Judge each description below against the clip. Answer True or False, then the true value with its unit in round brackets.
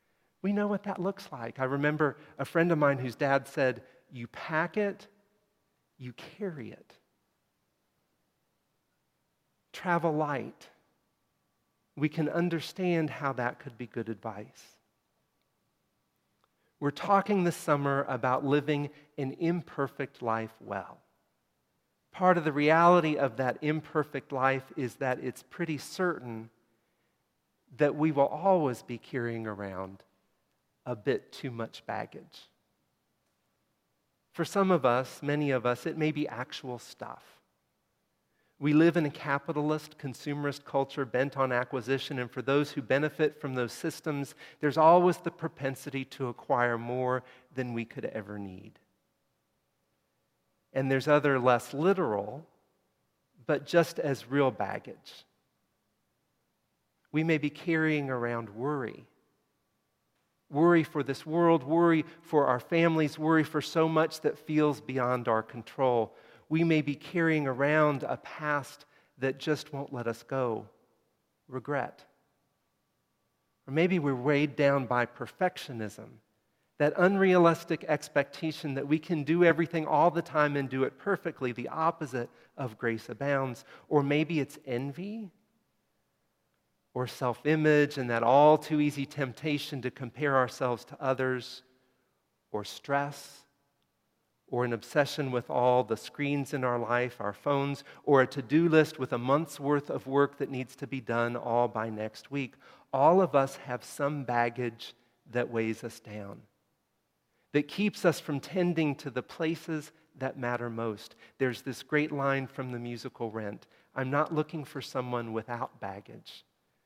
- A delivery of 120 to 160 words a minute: True (140 wpm)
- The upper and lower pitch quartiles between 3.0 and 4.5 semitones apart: True (3.8 semitones)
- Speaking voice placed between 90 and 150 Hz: True (140 Hz)